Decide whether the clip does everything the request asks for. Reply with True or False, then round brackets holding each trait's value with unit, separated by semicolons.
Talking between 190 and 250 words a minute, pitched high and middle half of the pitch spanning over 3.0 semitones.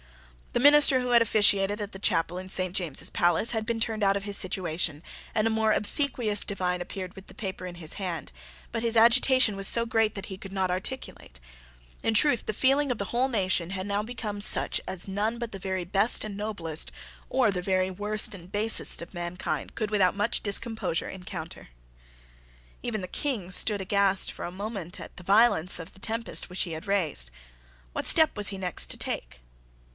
True (200 wpm; 200 Hz; 3.4 semitones)